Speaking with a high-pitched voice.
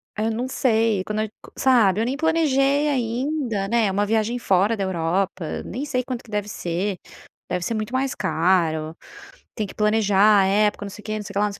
Yes: high, 215 Hz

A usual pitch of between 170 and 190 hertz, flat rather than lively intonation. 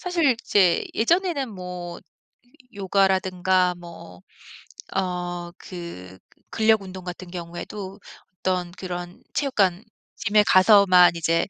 Yes: medium, 185 Hz; narrow, 2.3 semitones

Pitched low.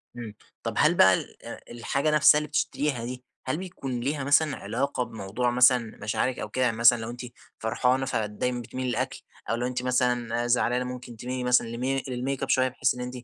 Yes: low, 125 Hz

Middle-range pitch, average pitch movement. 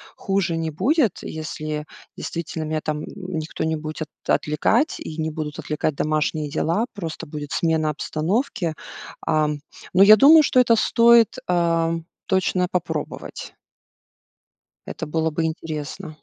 Yes: medium, 160 Hz; average, 3.5 semitones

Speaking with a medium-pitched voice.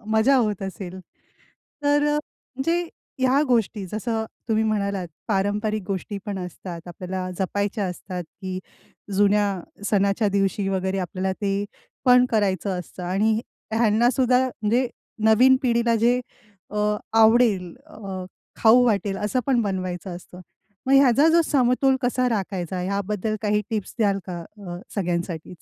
No: high, 205 Hz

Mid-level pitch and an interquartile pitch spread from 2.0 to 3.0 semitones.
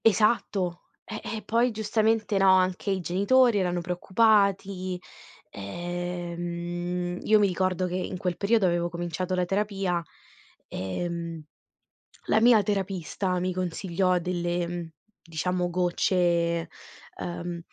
Yes: medium, 180 Hz; narrow, 2.3 semitones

